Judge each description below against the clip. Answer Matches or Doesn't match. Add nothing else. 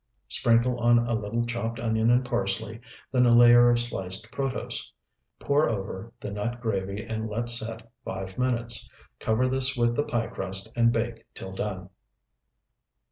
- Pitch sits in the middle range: Doesn't match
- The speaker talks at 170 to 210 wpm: Doesn't match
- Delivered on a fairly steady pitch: Matches